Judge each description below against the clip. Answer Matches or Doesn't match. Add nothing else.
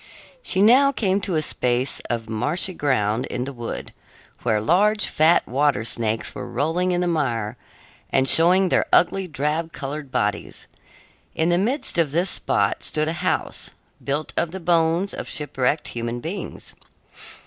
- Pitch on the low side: Doesn't match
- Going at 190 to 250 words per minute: Doesn't match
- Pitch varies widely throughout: Matches